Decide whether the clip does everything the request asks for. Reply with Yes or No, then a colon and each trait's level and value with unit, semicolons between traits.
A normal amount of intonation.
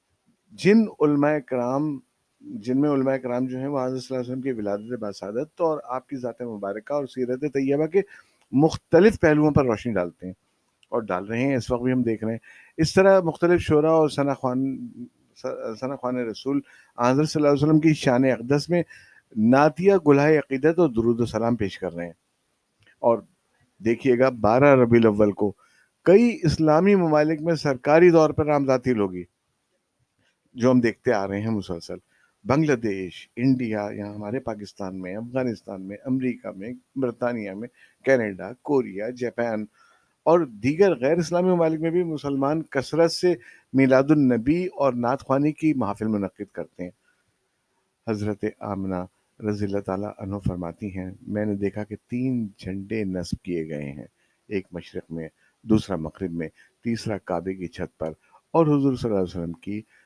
No: wide, 6.3 semitones